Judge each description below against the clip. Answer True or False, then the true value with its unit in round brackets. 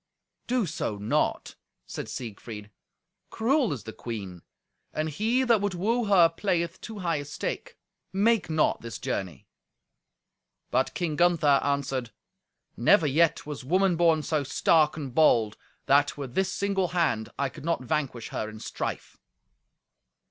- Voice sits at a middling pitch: True (155 Hz)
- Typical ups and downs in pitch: False (6.4 semitones)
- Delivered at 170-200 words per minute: False (145 wpm)